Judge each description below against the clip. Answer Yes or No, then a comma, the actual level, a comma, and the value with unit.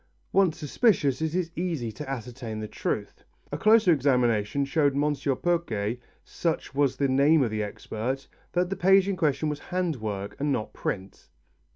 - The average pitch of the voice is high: No, medium, 140 Hz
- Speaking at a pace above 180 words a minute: No, average, 170 wpm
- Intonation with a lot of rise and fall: Yes, wide, 5.8 semitones